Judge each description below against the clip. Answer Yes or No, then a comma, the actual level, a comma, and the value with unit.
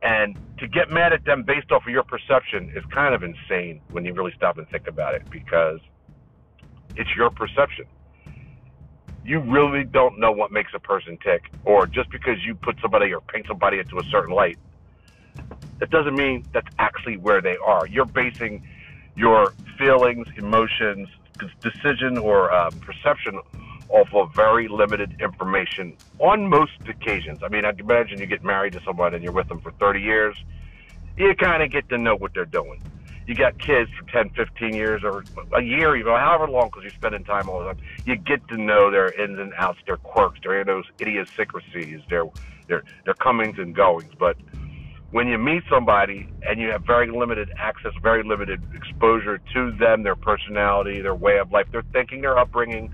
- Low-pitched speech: Yes, low, 105 Hz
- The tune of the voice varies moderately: No, wide, 5.7 semitones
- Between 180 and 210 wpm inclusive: Yes, average, 185 wpm